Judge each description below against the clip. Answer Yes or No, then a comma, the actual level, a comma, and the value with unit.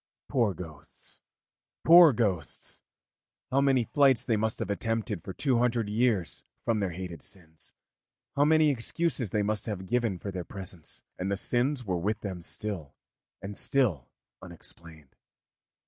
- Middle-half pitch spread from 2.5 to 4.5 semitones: No, average, 5.1 semitones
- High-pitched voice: No, low, 105 Hz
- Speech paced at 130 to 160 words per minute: Yes, average, 145 wpm